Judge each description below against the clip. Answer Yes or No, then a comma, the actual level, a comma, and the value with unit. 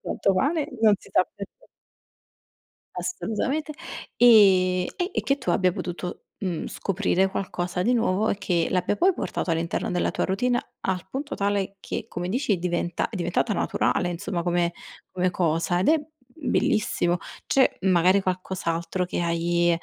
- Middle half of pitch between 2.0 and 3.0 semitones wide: No, average, 3.6 semitones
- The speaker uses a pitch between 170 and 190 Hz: Yes, medium, 185 Hz